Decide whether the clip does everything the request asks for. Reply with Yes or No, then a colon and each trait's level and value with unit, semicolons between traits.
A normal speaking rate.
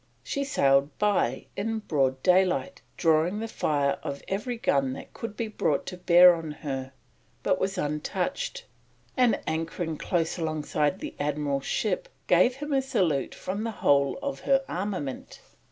Yes: average, 155 wpm